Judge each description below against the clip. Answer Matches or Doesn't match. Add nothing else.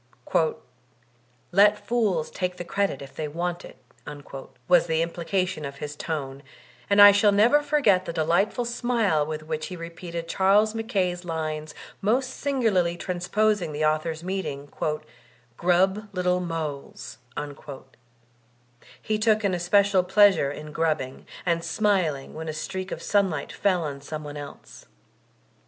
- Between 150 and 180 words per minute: Doesn't match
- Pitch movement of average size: Matches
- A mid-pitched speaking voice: Matches